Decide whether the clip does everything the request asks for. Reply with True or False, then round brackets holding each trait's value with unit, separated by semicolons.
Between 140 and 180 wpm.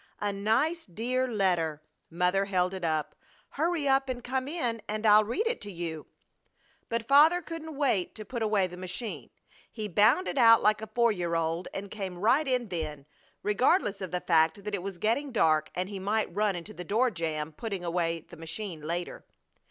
False (190 wpm)